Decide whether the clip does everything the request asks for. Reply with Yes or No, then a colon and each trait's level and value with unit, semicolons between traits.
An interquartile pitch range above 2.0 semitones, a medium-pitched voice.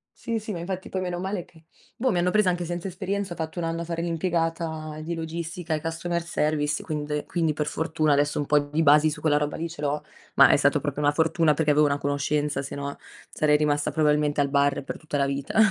Yes: narrow, 2.5 semitones; medium, 155 Hz